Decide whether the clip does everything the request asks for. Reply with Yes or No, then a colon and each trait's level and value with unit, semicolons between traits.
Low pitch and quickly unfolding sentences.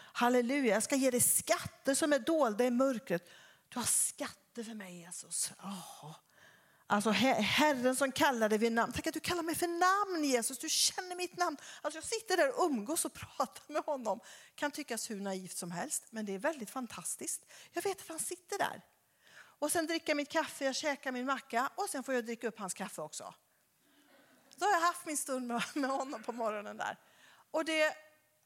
No: very high, 270 Hz; fast, 205 wpm